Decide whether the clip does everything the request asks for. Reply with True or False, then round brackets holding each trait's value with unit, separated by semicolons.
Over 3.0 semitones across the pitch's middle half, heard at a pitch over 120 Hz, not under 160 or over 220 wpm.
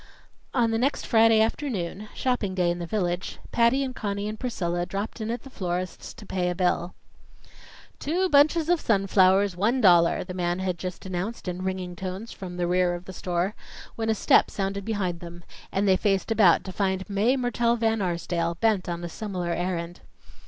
True (4.0 semitones; 190 Hz; 190 wpm)